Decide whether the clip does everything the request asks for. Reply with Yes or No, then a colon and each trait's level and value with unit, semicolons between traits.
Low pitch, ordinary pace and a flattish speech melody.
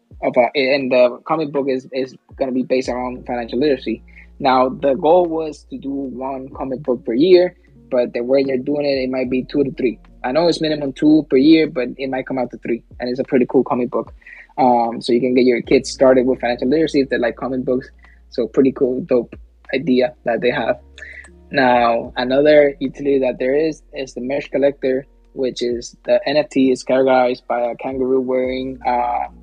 No: low, 130 Hz; fast, 210 wpm; narrow, 2.0 semitones